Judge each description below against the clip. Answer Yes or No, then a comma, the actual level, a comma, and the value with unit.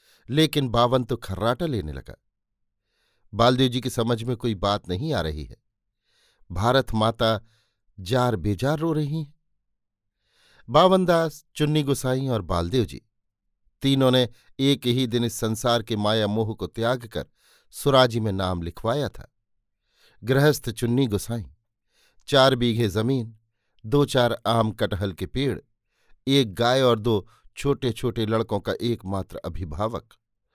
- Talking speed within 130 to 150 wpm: Yes, average, 140 wpm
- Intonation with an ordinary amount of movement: Yes, average, 3.6 semitones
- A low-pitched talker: Yes, low, 115 Hz